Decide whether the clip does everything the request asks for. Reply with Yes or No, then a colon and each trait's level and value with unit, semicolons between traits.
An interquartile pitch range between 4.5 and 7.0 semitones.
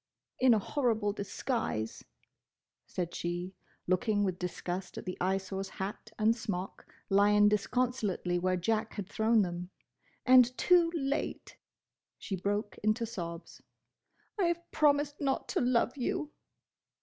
Yes: average, 5.2 semitones